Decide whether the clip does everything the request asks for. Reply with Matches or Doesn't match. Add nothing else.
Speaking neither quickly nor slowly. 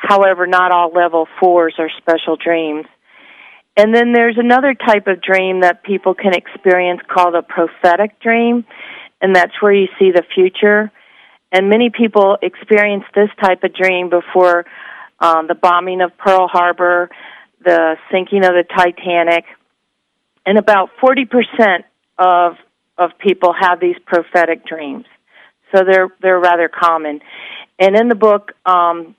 Matches